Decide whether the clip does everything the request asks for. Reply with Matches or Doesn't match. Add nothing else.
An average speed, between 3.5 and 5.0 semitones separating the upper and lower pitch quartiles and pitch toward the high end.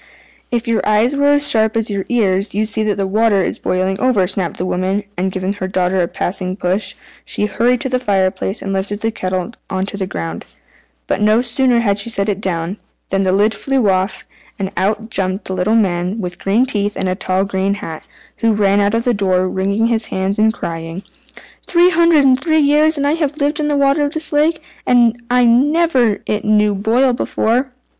Doesn't match